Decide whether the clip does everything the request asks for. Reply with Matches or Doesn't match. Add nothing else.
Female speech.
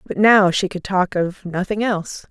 Matches